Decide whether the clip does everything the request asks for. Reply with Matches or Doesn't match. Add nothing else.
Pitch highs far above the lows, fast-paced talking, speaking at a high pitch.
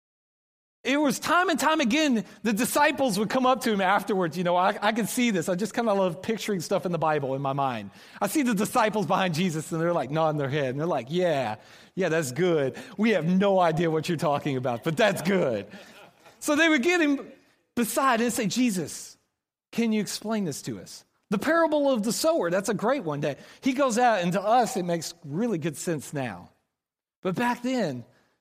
Matches